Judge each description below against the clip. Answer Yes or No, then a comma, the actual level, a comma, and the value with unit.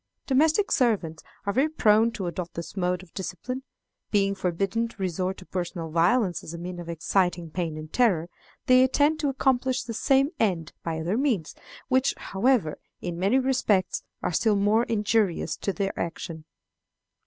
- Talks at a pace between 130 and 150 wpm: No, average, 165 wpm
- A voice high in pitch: Yes, high, 195 Hz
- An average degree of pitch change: No, wide, 6.3 semitones